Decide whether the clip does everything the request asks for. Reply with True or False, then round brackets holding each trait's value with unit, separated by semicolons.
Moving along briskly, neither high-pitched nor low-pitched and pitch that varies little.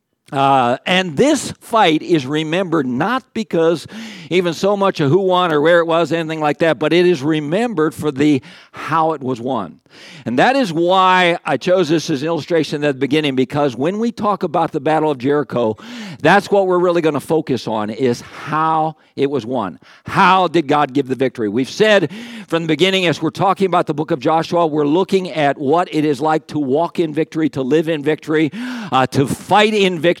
False (210 wpm; 160 Hz; 3.7 semitones)